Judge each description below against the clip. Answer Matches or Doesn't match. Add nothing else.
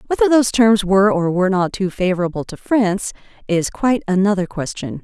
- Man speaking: Doesn't match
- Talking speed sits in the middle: Matches